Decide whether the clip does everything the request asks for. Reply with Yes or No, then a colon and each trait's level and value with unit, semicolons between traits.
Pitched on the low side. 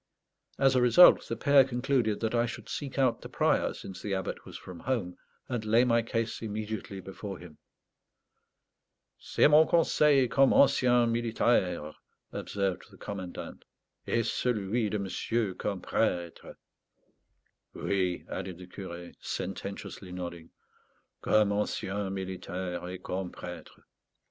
Yes: low, 105 Hz